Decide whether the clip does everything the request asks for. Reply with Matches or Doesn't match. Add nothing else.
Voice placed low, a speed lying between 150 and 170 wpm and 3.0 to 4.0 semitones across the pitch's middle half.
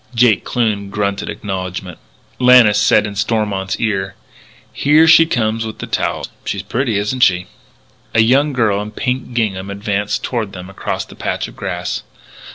Matches